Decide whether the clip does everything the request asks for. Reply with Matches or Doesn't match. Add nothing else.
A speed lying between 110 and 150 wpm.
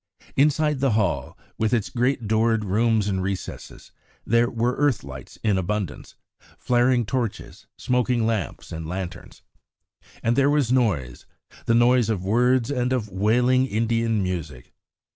Matches